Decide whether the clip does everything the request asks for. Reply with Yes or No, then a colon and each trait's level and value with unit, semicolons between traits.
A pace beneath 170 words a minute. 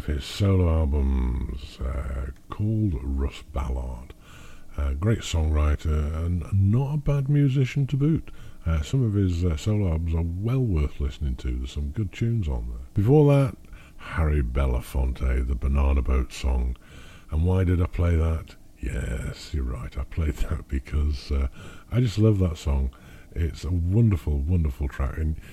Yes: average, 160 wpm